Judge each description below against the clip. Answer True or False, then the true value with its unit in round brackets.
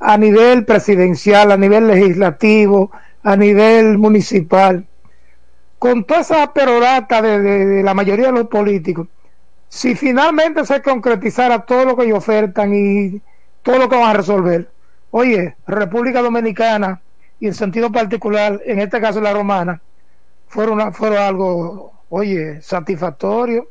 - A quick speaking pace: False (140 wpm)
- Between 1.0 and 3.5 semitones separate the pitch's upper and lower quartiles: True (3.2 semitones)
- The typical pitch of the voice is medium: False (210 Hz)